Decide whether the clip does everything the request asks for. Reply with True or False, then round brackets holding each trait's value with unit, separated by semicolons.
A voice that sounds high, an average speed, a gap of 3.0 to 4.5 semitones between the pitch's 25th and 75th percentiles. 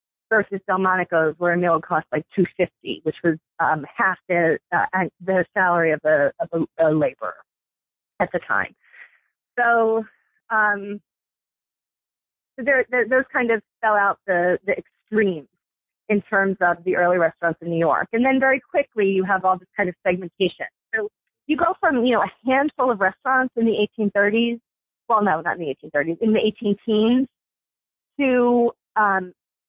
False (200 Hz; 175 wpm; 5.2 semitones)